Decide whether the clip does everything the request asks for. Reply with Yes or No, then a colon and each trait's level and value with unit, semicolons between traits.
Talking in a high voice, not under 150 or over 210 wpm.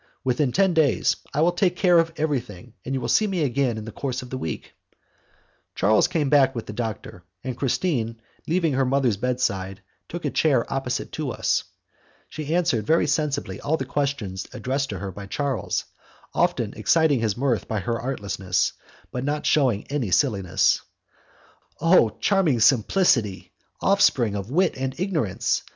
No: low, 130 Hz; average, 170 wpm